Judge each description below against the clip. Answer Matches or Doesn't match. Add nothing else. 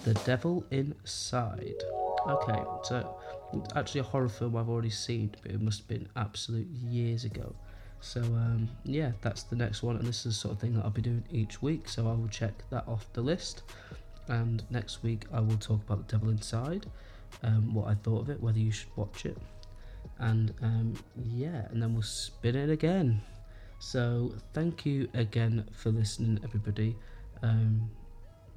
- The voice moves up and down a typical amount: Doesn't match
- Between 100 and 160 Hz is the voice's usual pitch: Matches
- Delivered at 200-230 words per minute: Doesn't match